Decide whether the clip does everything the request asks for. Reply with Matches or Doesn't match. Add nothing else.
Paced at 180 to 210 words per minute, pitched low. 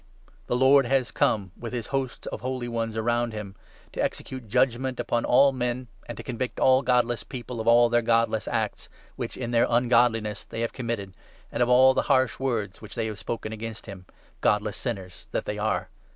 Matches